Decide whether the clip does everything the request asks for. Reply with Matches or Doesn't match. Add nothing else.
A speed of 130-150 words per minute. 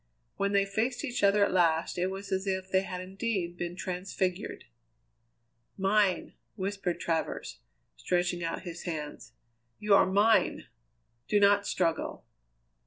Matches